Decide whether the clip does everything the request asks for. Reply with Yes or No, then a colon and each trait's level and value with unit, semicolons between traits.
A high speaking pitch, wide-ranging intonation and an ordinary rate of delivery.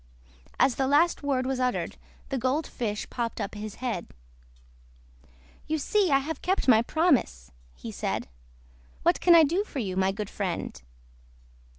Yes: very high, 255 Hz; wide, 6.5 semitones; average, 160 wpm